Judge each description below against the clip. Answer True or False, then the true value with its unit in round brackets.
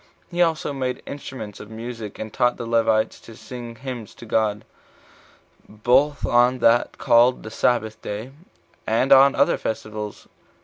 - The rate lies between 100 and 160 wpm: True (145 wpm)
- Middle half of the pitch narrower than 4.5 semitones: True (2.7 semitones)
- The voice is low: True (115 Hz)